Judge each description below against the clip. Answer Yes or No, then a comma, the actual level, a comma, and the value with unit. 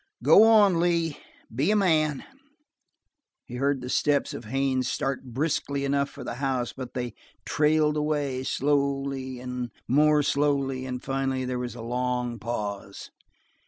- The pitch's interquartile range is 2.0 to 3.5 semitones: Yes, average, 2.8 semitones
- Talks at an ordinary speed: Yes, average, 145 wpm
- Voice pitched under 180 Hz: Yes, low, 135 Hz